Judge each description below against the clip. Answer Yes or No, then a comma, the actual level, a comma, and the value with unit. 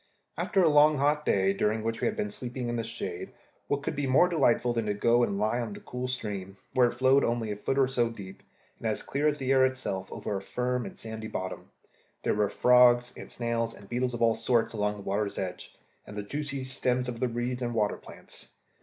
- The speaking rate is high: Yes, fast, 235 wpm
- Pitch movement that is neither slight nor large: Yes, average, 3.4 semitones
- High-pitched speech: No, low, 120 Hz